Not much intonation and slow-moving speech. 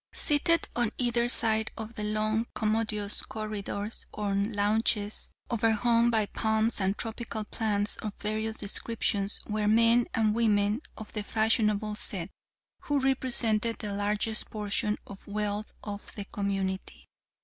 Yes: narrow, 1.7 semitones; slow, 130 wpm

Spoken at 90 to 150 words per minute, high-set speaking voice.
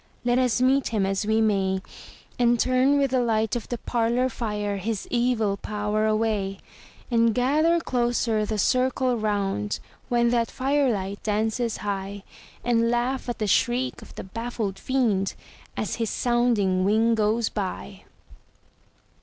Yes: average, 145 wpm; high, 225 Hz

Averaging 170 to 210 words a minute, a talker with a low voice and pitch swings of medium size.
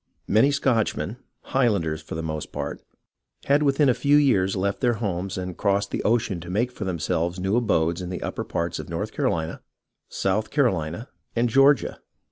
No: average, 175 wpm; low, 100 Hz; wide, 5.9 semitones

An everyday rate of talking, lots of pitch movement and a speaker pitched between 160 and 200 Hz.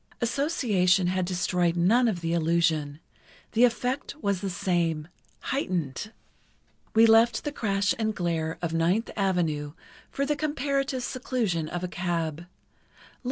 No: slow, 125 wpm; wide, 5.7 semitones; medium, 185 Hz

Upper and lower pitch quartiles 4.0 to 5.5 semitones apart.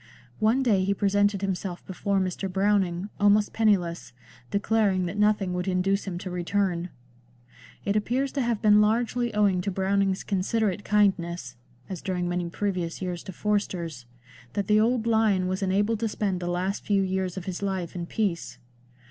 No: narrow, 2.5 semitones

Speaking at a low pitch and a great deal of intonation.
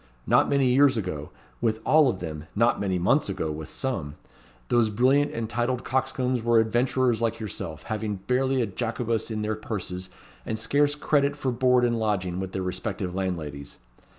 No: low, 110 Hz; average, 5.0 semitones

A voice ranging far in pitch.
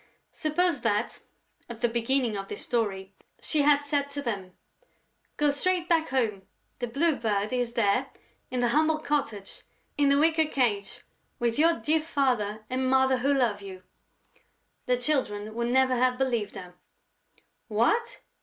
No: average, 5.0 semitones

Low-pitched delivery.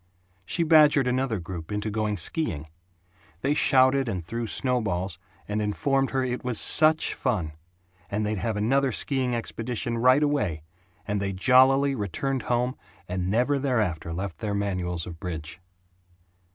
Yes: low, 115 Hz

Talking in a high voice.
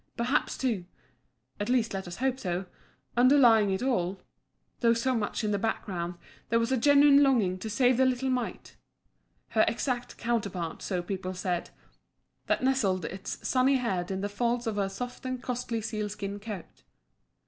Yes: high, 225 Hz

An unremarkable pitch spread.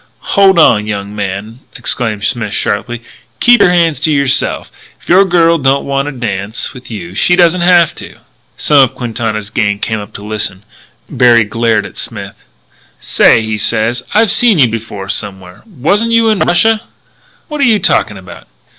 No: wide, 8.4 semitones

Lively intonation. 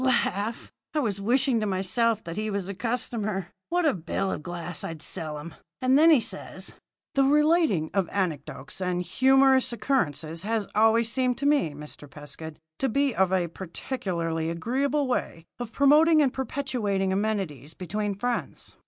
Yes: wide, 7.0 semitones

